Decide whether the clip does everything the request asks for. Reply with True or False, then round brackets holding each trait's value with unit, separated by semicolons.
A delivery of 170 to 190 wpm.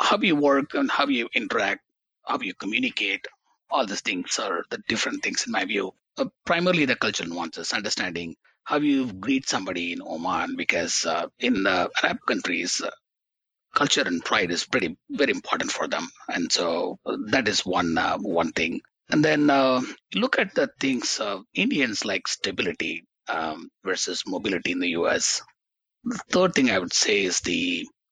True (175 wpm)